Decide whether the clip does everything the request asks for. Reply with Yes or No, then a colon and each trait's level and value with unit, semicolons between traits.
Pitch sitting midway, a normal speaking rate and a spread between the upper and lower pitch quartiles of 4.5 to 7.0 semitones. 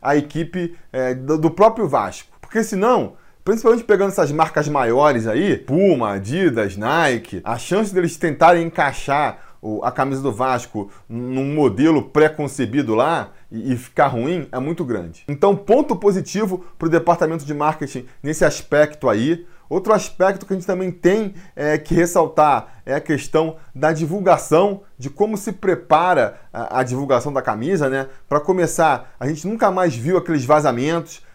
Yes: medium, 160 Hz; average, 155 wpm; wide, 5.4 semitones